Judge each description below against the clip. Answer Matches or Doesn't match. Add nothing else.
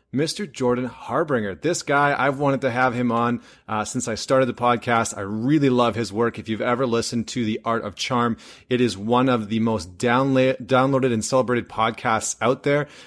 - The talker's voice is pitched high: Doesn't match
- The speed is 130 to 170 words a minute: Doesn't match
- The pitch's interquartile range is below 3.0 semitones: Matches